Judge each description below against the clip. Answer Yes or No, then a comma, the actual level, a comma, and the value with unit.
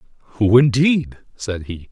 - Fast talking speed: No, slow, 125 wpm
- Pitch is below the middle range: Yes, low, 115 Hz